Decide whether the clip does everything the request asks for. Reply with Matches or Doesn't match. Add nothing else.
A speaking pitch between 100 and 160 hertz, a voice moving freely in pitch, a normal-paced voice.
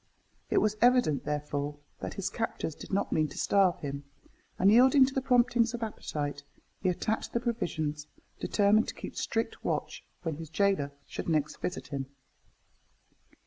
Doesn't match